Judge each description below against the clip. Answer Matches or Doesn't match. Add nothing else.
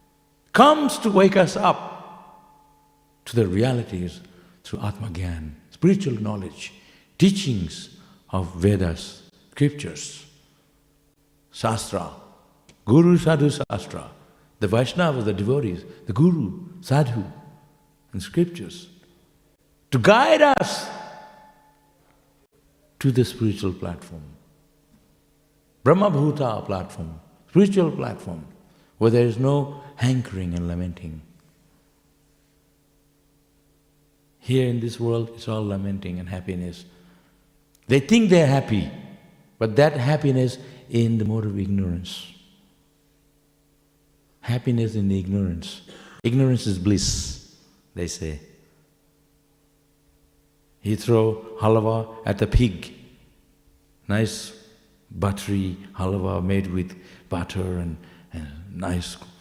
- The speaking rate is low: Matches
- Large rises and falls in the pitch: Matches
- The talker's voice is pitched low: Matches